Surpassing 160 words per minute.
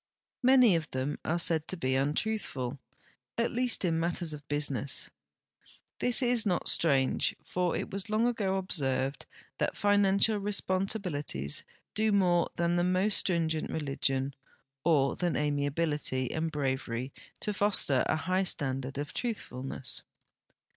No: average, 140 wpm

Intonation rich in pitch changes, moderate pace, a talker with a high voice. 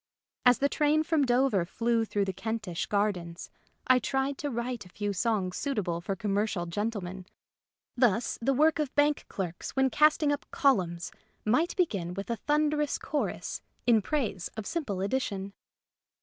Yes: wide, 6.4 semitones; average, 155 wpm; high, 230 Hz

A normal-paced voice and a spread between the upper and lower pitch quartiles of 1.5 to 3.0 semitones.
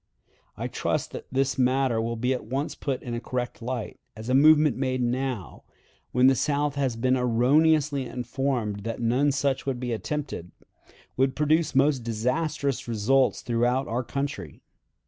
Yes: average, 160 wpm; narrow, 2.6 semitones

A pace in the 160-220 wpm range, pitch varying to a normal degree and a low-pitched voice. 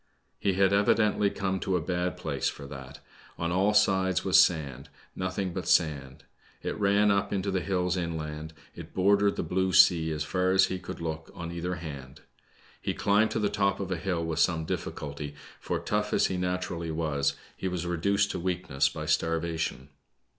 Yes: average, 190 wpm; average, 3.4 semitones; very low, 90 Hz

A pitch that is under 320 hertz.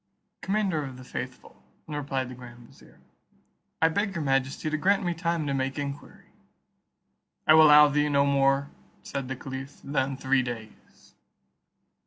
Yes: medium, 140 Hz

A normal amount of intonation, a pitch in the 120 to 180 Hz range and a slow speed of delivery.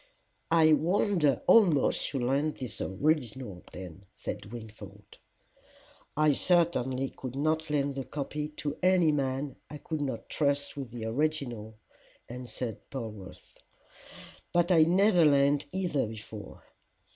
Yes: average, 4.5 semitones; medium, 140 Hz; slow, 120 wpm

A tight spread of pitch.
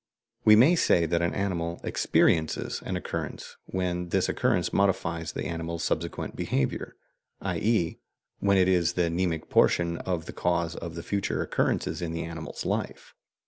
Yes: narrow, 1.9 semitones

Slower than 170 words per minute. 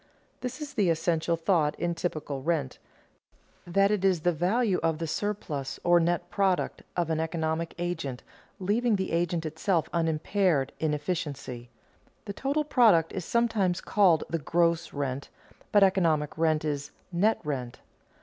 Yes: average, 150 wpm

